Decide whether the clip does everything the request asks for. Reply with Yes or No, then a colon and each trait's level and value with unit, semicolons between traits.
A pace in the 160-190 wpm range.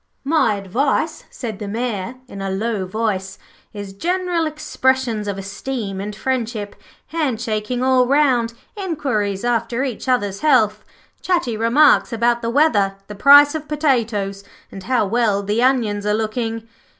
No: average, 145 wpm